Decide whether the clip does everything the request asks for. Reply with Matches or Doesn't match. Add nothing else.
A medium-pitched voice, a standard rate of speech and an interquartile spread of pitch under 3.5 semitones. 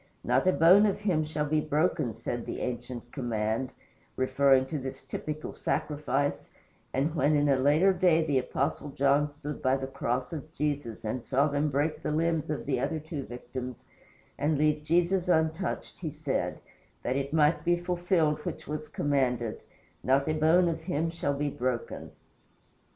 Matches